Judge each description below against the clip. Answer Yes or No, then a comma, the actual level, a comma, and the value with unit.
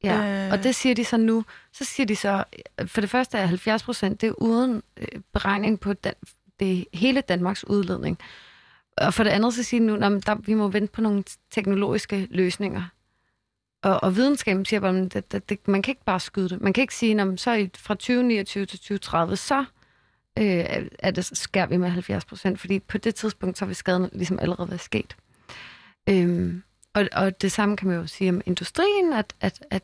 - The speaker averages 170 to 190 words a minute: Yes, average, 180 wpm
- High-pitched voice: Yes, high, 200 Hz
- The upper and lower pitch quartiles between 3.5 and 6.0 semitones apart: No, average, 2.9 semitones